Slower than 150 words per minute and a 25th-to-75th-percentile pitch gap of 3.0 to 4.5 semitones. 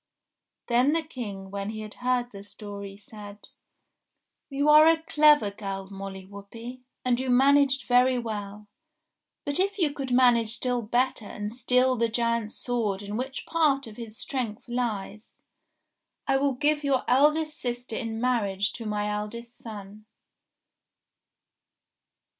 Yes: average, 140 wpm; average, 3.9 semitones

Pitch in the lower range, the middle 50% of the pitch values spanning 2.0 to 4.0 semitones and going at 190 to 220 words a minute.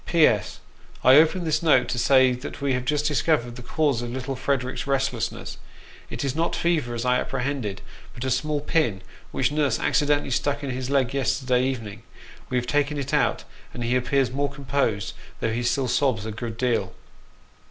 Yes: low, 130 Hz; average, 2.9 semitones; average, 195 wpm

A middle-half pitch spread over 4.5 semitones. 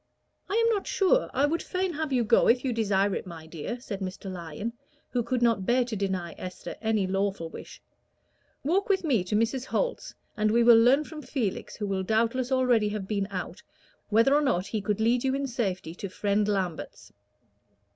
Yes: average, 4.9 semitones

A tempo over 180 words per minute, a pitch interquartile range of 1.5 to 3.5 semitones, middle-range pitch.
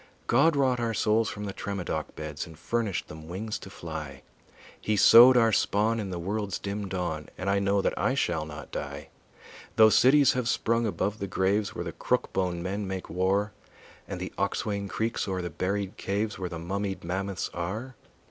No: average, 190 wpm; average, 3.2 semitones; low, 100 Hz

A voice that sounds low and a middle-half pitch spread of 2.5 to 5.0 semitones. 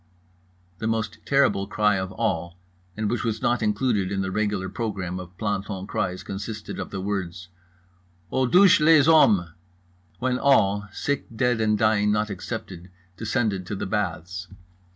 Yes: low, 105 Hz; average, 3.2 semitones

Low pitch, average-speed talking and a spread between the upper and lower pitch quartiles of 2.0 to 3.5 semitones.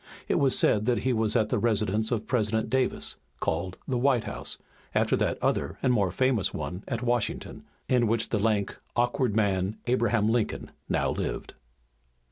Yes: low, 115 Hz; average, 170 wpm; average, 2.8 semitones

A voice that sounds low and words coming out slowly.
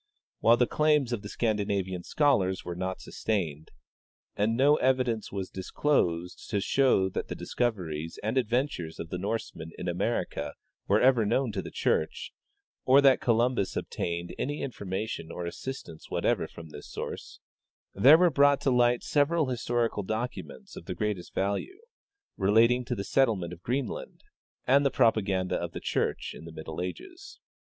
No: low, 110 Hz; average, 160 wpm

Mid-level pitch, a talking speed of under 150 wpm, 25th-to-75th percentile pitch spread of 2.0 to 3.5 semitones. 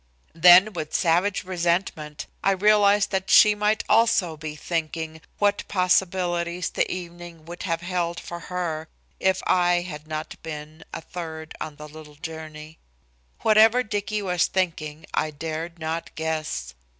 Yes: medium, 170 Hz; average, 140 wpm; average, 3.1 semitones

